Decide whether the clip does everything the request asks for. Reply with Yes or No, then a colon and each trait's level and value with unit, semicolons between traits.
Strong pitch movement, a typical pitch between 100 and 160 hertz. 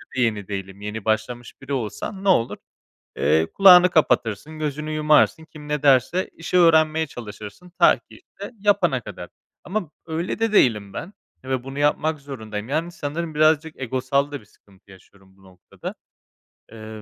Yes: wide, 6.6 semitones; medium, 140 Hz